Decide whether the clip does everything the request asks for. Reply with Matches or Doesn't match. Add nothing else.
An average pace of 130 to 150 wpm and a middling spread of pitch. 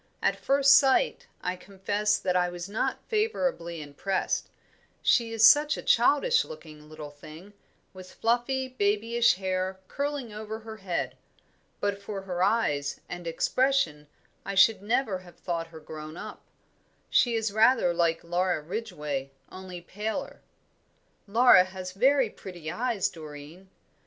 Matches